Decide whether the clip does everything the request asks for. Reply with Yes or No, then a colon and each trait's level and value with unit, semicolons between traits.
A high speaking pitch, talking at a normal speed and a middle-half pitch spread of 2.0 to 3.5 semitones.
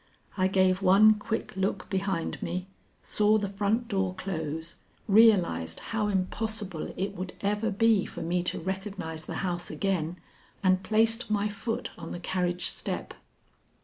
Yes: high, 195 Hz; average, 145 wpm; narrow, 2.5 semitones